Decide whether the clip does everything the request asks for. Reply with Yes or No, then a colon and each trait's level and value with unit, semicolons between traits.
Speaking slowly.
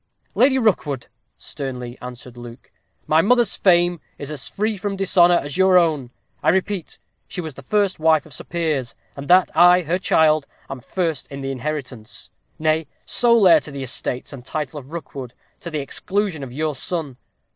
No: average, 180 wpm